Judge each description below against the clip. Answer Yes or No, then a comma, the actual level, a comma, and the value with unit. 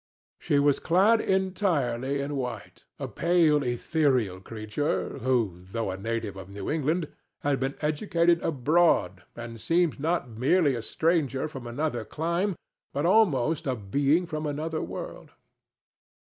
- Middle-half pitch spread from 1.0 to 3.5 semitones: No, wide, 5.6 semitones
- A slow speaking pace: Yes, slow, 130 wpm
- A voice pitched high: No, medium, 145 Hz